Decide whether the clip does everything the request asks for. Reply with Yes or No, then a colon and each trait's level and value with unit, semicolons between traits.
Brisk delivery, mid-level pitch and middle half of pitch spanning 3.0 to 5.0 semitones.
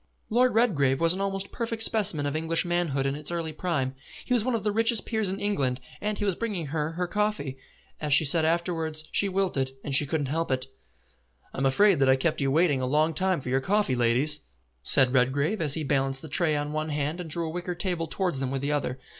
No: fast, 235 wpm; medium, 160 Hz; wide, 5.4 semitones